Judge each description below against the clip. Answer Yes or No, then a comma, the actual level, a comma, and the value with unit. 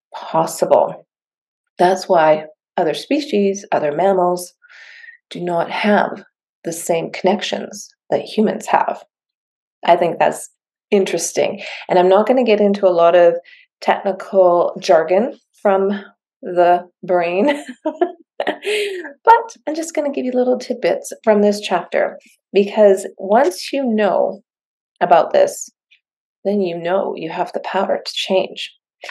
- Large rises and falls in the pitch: Yes, wide, 6.4 semitones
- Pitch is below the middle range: No, high, 200 Hz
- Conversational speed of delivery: No, slow, 130 wpm